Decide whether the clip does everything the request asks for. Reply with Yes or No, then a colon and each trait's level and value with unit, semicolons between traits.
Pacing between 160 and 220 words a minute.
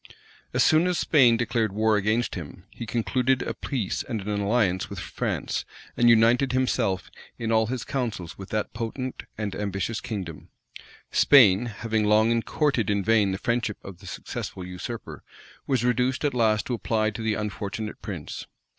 Yes: average, 165 wpm